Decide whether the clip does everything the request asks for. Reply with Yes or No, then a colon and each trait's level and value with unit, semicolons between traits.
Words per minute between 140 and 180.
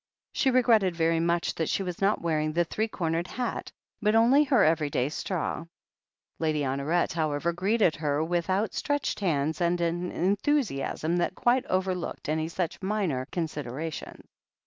Yes: average, 160 wpm